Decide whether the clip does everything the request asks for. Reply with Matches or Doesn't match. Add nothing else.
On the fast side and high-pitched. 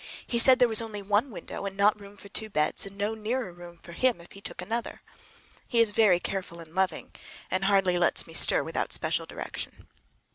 Matches